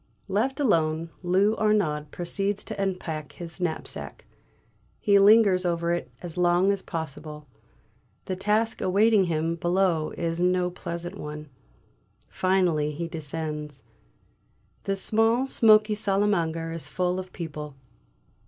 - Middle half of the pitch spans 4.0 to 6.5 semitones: No, average, 3.6 semitones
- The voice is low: No, medium, 180 Hz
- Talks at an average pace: No, slow, 125 wpm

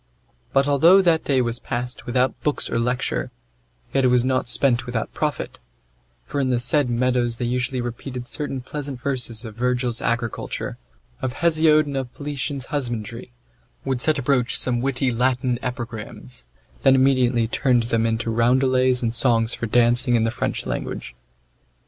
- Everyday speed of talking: Yes, average, 160 wpm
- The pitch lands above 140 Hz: No, low, 125 Hz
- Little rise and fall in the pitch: Yes, narrow, 2.2 semitones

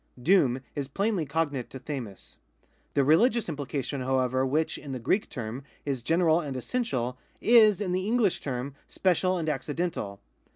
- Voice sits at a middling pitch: Yes, medium, 145 Hz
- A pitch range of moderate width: No, wide, 5.9 semitones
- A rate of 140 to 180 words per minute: Yes, average, 160 wpm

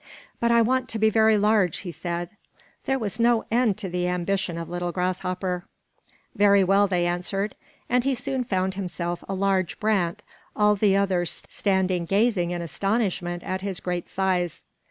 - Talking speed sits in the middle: Yes, average, 170 wpm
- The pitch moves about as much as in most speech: Yes, average, 3.2 semitones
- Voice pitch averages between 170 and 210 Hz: Yes, high, 190 Hz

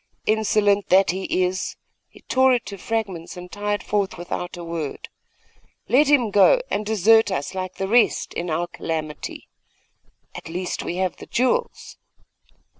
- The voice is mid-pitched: No, high, 195 Hz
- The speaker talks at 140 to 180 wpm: Yes, average, 155 wpm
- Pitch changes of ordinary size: Yes, average, 3.7 semitones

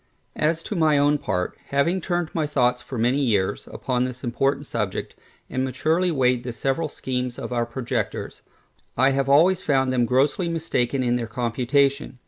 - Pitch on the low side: Yes, low, 130 Hz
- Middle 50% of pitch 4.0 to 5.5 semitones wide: No, average, 3.3 semitones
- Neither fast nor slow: Yes, average, 170 wpm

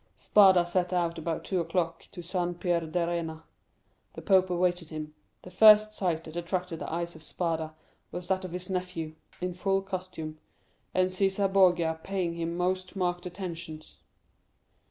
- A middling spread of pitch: No, narrow, 1.9 semitones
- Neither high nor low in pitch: Yes, medium, 175 Hz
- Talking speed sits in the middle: Yes, average, 155 wpm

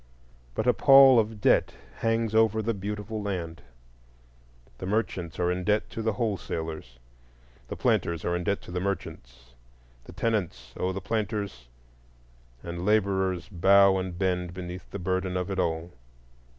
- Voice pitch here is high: No, very low, 95 Hz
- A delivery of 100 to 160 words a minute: Yes, average, 150 wpm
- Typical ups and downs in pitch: Yes, average, 3.2 semitones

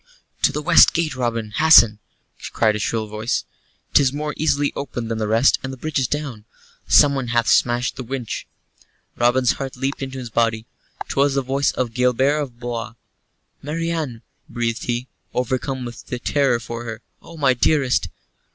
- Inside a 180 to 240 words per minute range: No, average, 165 wpm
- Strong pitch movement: No, average, 3.1 semitones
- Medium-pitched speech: No, low, 125 Hz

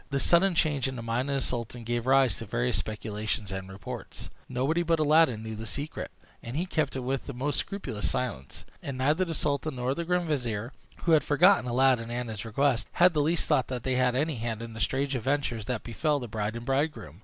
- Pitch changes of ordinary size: Yes, average, 4.3 semitones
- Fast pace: Yes, fast, 225 wpm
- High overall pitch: No, low, 130 Hz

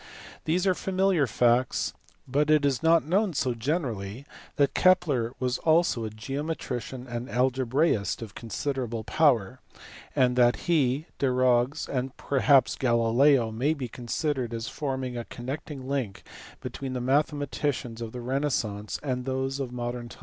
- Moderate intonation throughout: Yes, average, 3.3 semitones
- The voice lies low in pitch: Yes, low, 130 Hz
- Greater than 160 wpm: No, average, 140 wpm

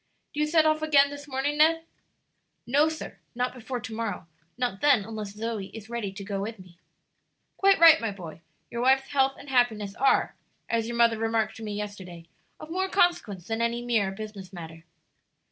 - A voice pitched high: Yes, high, 230 Hz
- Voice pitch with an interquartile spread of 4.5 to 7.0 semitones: Yes, wide, 5.5 semitones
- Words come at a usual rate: Yes, average, 190 wpm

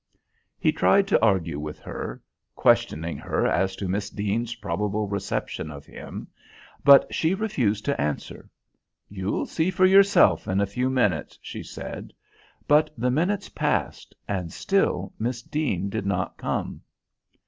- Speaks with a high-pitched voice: No, low, 105 Hz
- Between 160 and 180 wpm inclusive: No, average, 145 wpm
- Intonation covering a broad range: Yes, wide, 7.6 semitones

